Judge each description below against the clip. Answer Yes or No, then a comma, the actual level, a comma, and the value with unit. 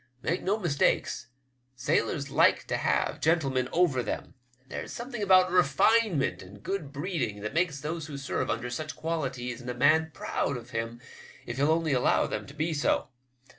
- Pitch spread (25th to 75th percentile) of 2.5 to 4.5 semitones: No, average, 5.0 semitones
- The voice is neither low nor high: Yes, medium, 145 Hz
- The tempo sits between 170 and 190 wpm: Yes, average, 180 wpm